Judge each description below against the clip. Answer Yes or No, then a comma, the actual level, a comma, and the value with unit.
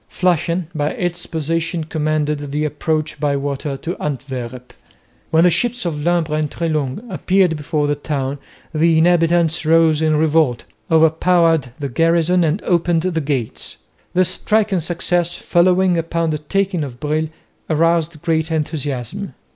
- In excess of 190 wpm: No, average, 145 wpm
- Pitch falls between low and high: Yes, medium, 160 Hz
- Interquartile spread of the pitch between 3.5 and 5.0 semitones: No, narrow, 2.6 semitones